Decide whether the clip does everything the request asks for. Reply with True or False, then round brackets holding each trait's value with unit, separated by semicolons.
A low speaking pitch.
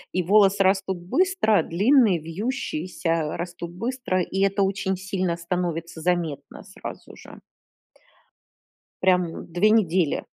False (185 Hz)